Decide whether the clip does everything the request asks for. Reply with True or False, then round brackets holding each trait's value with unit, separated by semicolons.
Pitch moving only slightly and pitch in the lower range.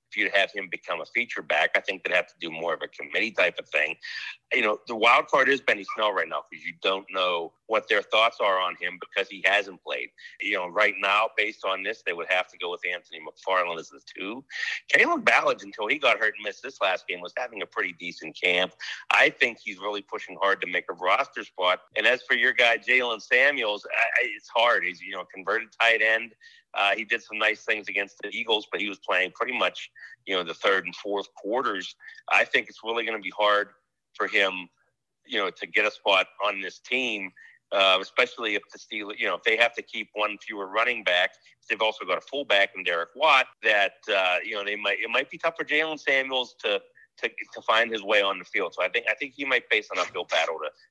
False (4.3 semitones; 110 Hz)